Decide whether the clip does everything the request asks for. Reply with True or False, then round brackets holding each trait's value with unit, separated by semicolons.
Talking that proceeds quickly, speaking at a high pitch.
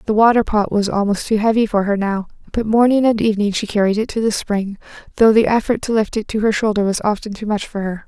True (260 wpm; 210 Hz)